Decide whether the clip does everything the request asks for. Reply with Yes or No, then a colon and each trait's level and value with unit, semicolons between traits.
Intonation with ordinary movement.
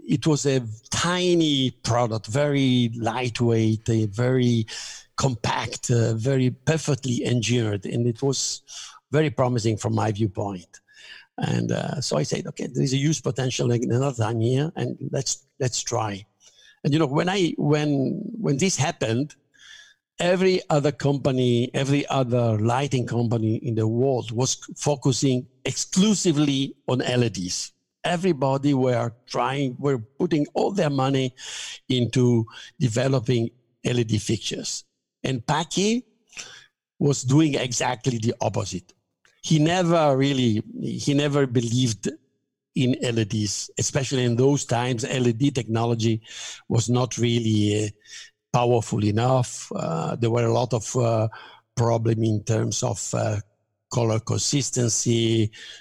Yes: average, 3.6 semitones